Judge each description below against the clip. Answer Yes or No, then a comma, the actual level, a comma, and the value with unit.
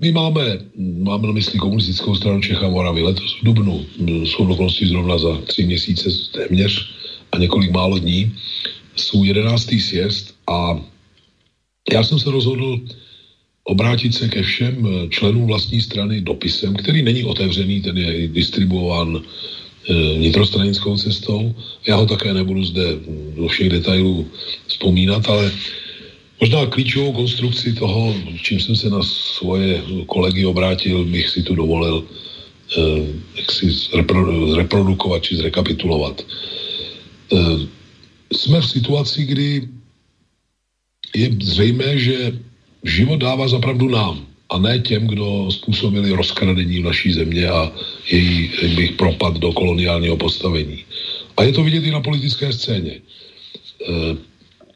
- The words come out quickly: No, average, 125 wpm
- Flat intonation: No, average, 4.3 semitones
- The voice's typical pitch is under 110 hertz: Yes, very low, 95 Hz